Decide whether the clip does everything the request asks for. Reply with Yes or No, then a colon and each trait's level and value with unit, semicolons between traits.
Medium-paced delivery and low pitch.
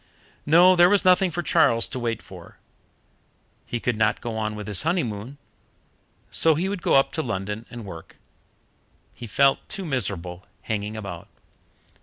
Yes: average, 160 wpm; low, 120 Hz